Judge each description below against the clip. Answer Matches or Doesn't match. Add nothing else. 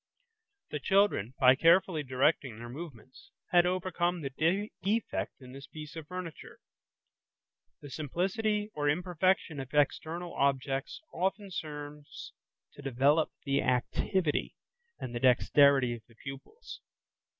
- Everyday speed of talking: Doesn't match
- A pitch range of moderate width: Matches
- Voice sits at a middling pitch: Matches